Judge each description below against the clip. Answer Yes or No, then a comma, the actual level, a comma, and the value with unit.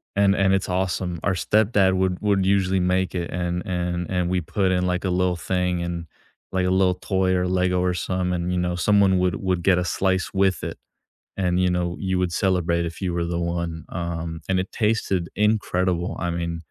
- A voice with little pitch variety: Yes, narrow, 1.3 semitones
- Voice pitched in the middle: No, very low, 90 Hz